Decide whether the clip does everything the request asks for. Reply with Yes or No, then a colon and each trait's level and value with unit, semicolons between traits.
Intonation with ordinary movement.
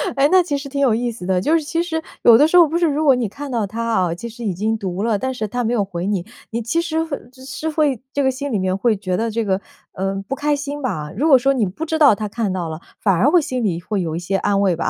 No: wide, 6.6 semitones